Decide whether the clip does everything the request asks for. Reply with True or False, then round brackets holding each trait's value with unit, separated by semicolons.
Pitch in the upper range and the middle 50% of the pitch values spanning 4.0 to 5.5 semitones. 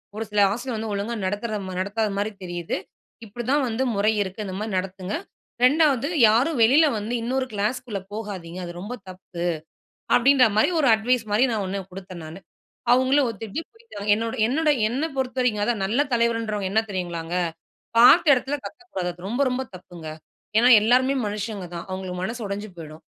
True (215 Hz; 4.7 semitones)